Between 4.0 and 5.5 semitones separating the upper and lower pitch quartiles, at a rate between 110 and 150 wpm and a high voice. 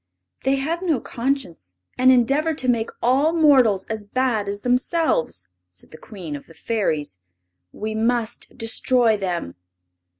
Yes: average, 4.9 semitones; average, 140 wpm; high, 230 Hz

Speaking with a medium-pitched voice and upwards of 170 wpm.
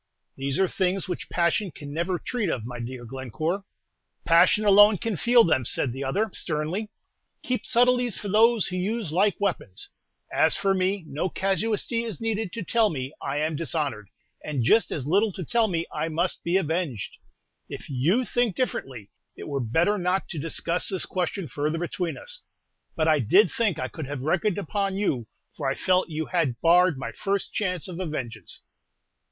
Yes: medium, 175 Hz; average, 185 wpm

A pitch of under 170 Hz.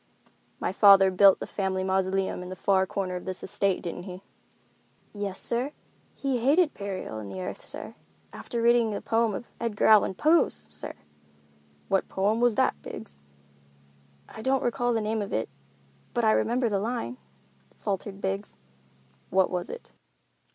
No: high, 200 Hz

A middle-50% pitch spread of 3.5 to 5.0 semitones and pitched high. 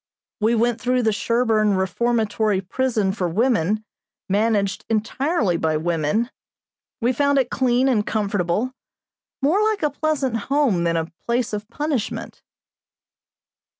Yes: average, 4.3 semitones; high, 225 Hz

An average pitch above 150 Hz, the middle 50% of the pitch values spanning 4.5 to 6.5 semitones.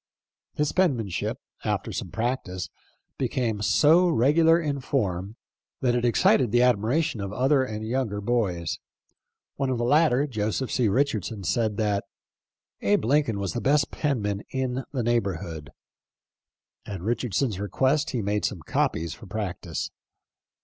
No: low, 115 Hz; average, 4.9 semitones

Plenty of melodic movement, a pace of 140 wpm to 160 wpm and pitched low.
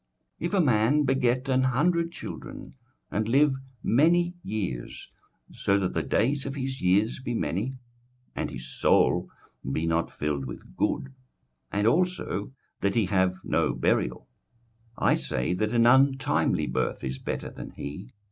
Yes: wide, 6.7 semitones; average, 150 wpm; low, 115 Hz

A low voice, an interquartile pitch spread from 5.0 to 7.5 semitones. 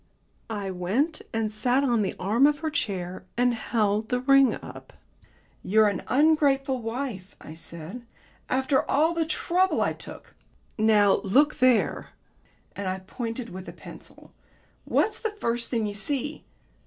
No: high, 235 Hz; average, 5.3 semitones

